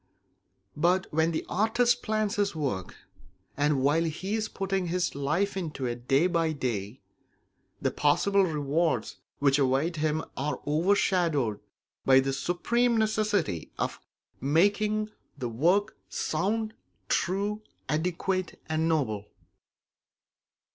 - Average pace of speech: No, slow, 115 wpm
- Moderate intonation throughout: No, wide, 5.9 semitones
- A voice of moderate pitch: Yes, medium, 165 Hz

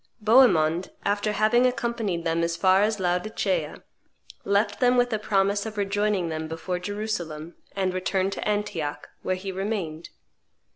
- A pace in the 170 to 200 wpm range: No, average, 145 wpm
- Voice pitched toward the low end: No, high, 195 Hz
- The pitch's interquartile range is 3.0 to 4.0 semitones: Yes, average, 3.3 semitones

